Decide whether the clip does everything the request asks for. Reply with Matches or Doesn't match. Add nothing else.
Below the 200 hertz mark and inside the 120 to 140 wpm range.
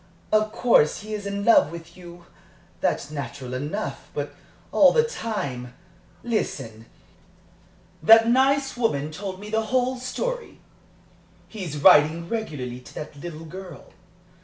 Matches